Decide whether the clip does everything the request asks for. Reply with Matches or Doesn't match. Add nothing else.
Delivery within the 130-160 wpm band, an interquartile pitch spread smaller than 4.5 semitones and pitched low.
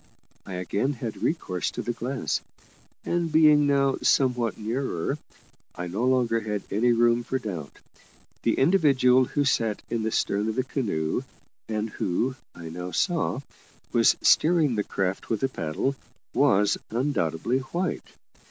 Doesn't match